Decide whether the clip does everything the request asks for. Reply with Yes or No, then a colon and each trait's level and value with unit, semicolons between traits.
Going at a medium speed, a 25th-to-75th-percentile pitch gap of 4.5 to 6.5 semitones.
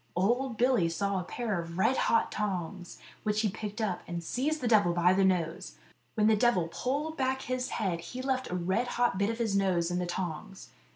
No: fast, 215 wpm; wide, 5.4 semitones